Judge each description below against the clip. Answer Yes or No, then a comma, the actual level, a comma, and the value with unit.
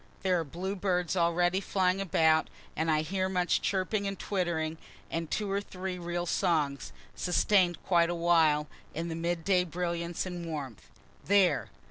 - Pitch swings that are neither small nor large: No, narrow, 2.2 semitones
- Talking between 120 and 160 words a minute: Yes, average, 150 wpm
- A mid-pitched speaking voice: Yes, medium, 175 Hz